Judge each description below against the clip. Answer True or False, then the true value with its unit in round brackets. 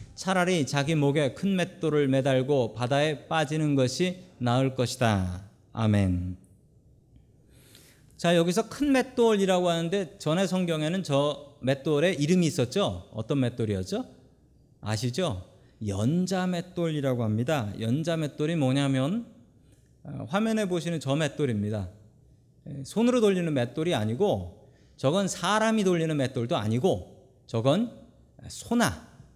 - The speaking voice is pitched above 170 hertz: False (145 Hz)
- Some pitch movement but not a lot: False (6.3 semitones)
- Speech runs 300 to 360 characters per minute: False (260 characters per minute)